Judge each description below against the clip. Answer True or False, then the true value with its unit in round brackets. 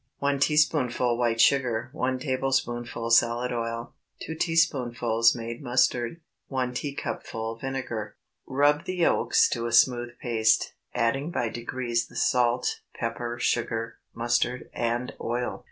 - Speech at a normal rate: False (120 wpm)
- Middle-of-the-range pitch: False (120 Hz)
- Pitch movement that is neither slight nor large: False (2.1 semitones)